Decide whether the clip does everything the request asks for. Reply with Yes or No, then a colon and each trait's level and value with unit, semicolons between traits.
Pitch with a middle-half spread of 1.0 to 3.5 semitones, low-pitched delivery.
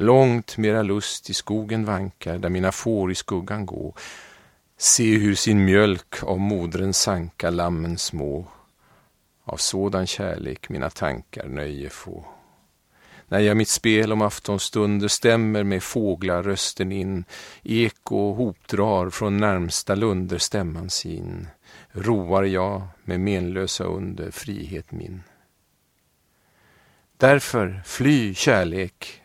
Yes: narrow, 2.6 semitones; very low, 95 Hz